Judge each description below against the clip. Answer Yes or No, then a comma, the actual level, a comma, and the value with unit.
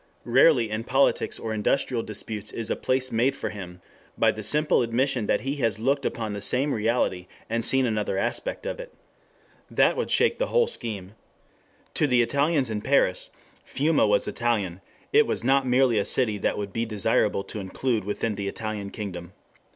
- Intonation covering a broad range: No, average, 4.3 semitones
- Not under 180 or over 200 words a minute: Yes, average, 190 wpm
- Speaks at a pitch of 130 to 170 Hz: No, low, 115 Hz